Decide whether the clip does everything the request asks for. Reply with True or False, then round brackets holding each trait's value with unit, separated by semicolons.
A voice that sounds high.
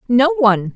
True (260 Hz)